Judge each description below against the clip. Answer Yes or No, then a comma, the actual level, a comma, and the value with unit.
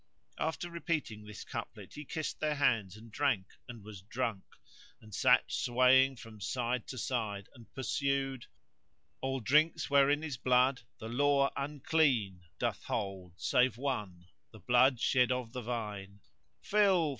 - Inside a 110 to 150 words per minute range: Yes, average, 145 wpm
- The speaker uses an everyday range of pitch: Yes, average, 4.5 semitones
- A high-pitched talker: No, low, 125 Hz